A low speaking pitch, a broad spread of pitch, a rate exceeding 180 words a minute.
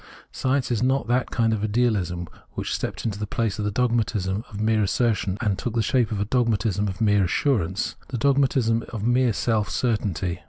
No: low, 110 Hz; average, 3.2 semitones; average, 195 wpm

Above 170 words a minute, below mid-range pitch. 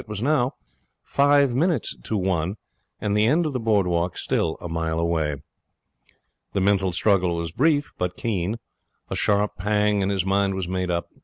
Yes: average, 180 wpm; low, 100 Hz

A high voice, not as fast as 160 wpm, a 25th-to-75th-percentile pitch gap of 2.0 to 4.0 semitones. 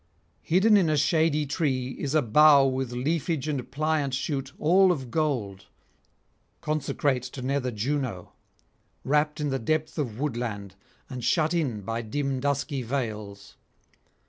No: medium, 140 Hz; average, 140 wpm; average, 3.7 semitones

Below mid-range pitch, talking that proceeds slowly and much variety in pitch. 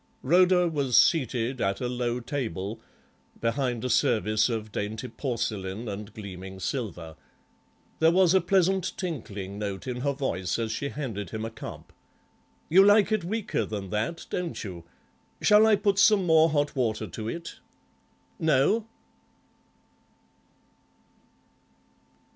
Yes: low, 125 Hz; slow, 130 wpm; wide, 7.8 semitones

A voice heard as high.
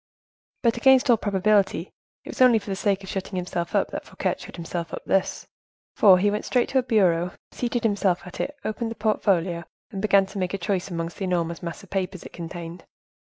Yes: high, 195 Hz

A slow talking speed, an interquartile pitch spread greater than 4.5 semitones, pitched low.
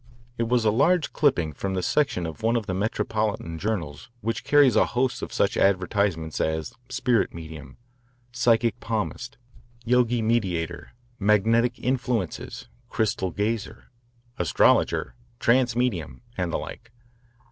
Yes: slow, 130 wpm; wide, 5.4 semitones; low, 110 Hz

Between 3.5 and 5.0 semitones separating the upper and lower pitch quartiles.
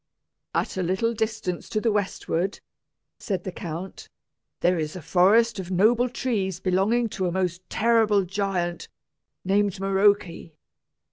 No: average, 2.9 semitones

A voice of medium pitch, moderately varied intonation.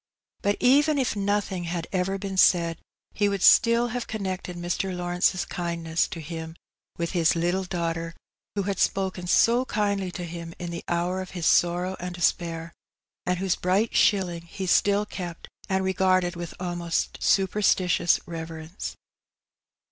No: medium, 180 Hz; narrow, 2.3 semitones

